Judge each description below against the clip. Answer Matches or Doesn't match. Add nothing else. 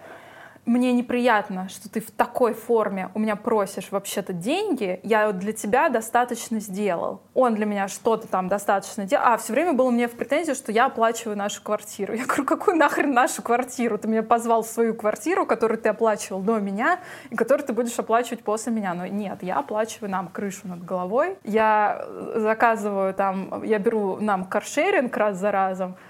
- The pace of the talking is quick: Matches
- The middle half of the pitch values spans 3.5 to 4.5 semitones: Doesn't match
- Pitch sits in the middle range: Doesn't match